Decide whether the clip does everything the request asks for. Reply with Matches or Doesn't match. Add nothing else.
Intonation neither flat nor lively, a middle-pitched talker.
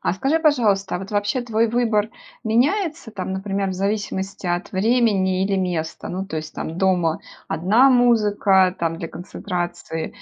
Doesn't match